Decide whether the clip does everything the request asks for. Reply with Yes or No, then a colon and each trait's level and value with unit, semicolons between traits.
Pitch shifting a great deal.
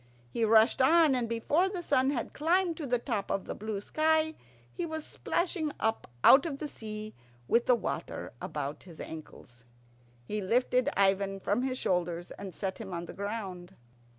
Yes: wide, 7.0 semitones